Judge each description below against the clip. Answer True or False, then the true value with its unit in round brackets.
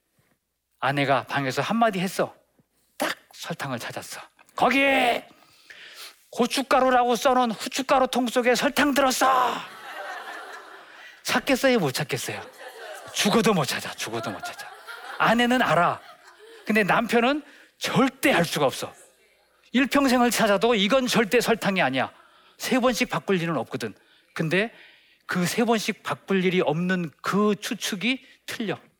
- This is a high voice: True (240 Hz)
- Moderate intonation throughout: True (5.0 semitones)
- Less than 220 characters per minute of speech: False (260 characters per minute)